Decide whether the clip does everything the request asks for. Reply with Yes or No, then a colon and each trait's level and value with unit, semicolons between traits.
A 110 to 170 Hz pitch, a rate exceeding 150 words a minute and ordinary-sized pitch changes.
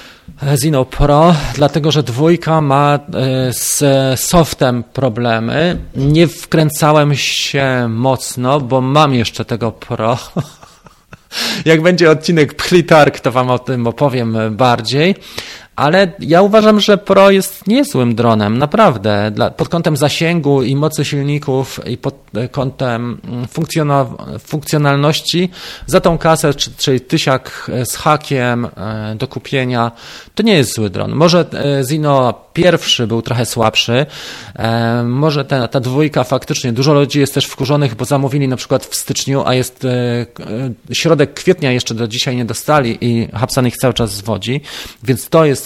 No: low, 135 Hz; average, 135 wpm; average, 4.1 semitones